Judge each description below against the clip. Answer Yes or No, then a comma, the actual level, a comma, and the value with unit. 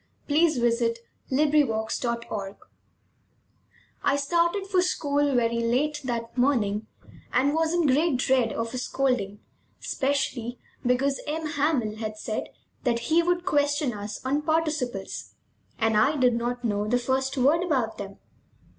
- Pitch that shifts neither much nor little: Yes, average, 4.4 semitones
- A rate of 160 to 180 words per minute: No, average, 145 wpm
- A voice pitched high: Yes, very high, 260 Hz